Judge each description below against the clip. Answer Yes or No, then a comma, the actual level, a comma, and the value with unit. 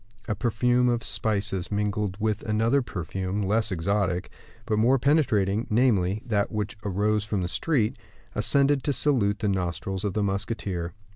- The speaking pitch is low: Yes, low, 105 Hz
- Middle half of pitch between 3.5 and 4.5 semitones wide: No, average, 2.9 semitones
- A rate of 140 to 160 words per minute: Yes, average, 150 wpm